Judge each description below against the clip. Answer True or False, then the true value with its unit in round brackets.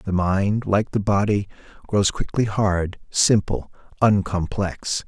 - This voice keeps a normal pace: False (120 wpm)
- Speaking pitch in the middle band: False (100 Hz)